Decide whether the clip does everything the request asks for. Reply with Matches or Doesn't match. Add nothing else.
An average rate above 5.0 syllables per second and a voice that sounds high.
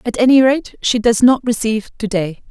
Matches